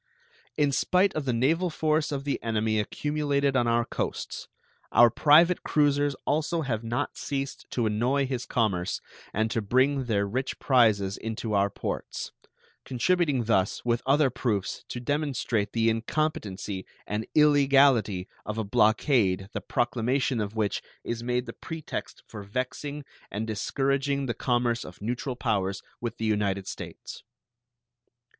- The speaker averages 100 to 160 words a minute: Yes, average, 145 wpm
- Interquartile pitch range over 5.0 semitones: No, average, 4.5 semitones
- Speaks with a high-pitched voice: No, low, 120 Hz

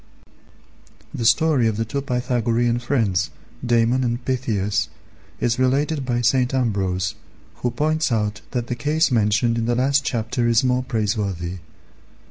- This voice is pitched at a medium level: No, low, 120 Hz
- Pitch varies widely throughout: No, average, 2.8 semitones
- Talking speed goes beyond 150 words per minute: No, average, 140 wpm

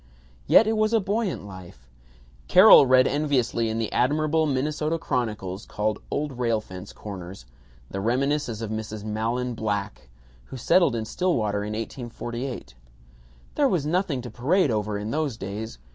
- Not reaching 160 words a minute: Yes, average, 150 wpm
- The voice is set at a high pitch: No, low, 120 Hz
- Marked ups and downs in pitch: Yes, wide, 5.8 semitones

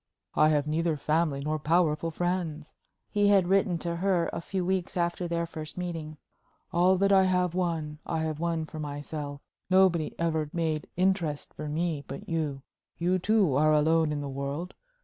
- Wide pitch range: No, average, 2.8 semitones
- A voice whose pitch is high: No, medium, 165 Hz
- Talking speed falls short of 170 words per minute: No, average, 175 wpm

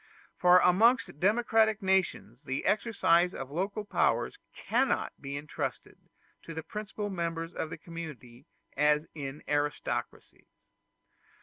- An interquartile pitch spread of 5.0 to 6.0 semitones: Yes, average, 5.3 semitones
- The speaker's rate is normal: No, slow, 115 wpm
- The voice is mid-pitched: Yes, medium, 170 Hz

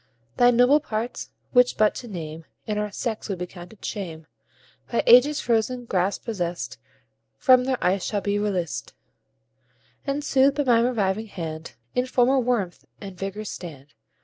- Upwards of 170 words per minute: No, average, 155 wpm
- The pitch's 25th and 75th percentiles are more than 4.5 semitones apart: Yes, average, 5.2 semitones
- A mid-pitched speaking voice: No, high, 215 Hz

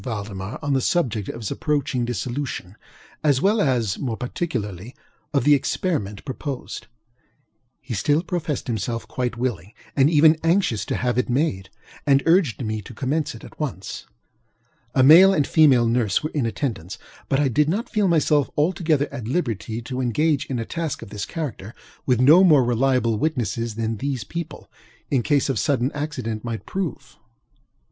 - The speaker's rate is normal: Yes, average, 170 wpm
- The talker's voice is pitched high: No, low, 130 Hz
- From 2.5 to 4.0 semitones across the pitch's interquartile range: No, average, 4.8 semitones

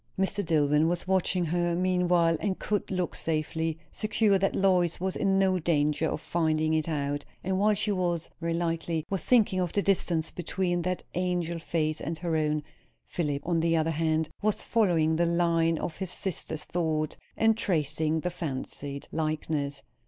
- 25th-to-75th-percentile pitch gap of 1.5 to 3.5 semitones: Yes, average, 2.7 semitones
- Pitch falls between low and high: Yes, medium, 170 Hz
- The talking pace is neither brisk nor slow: Yes, average, 165 wpm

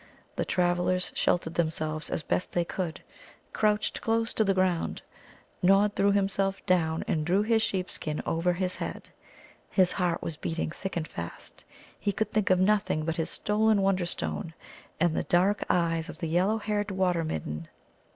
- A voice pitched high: No, medium, 180 Hz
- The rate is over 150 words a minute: Yes, average, 170 wpm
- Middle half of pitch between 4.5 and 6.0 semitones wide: No, average, 3.4 semitones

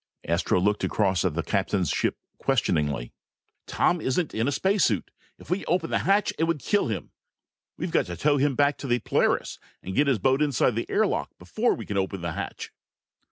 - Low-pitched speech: Yes, low, 125 Hz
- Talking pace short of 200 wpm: No, fast, 205 wpm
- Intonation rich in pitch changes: Yes, wide, 8.5 semitones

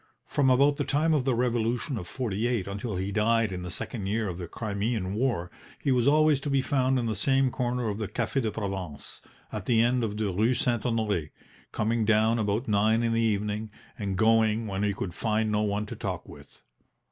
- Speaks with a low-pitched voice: Yes, low, 110 Hz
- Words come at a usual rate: No, fast, 215 wpm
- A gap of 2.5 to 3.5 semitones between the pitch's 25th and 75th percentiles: Yes, average, 3.2 semitones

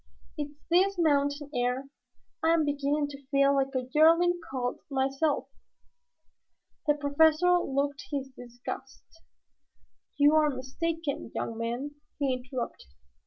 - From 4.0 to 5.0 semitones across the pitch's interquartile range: No, narrow, 2.5 semitones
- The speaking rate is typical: No, slow, 120 wpm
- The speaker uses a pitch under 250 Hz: No, very high, 285 Hz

